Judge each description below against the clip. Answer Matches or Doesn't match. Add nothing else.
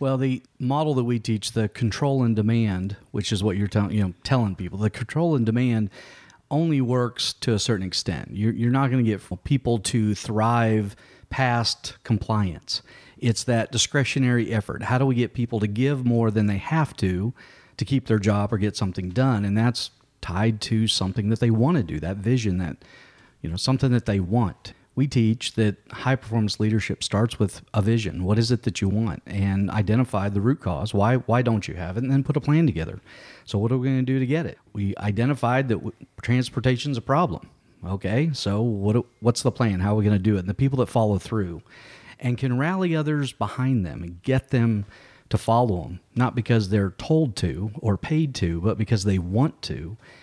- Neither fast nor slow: Doesn't match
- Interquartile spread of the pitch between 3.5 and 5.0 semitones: Matches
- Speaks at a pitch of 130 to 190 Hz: Doesn't match